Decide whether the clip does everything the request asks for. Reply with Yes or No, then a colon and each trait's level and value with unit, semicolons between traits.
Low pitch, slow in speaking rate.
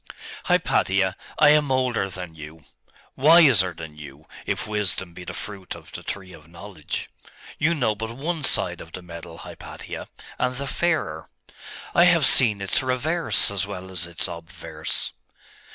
No: low, 100 Hz; average, 155 wpm